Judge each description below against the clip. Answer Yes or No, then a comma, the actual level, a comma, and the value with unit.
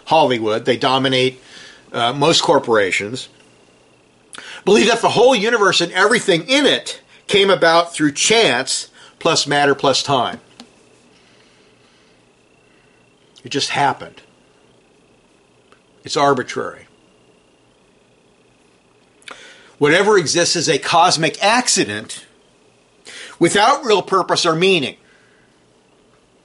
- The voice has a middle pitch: Yes, medium, 175 Hz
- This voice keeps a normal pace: No, slow, 90 wpm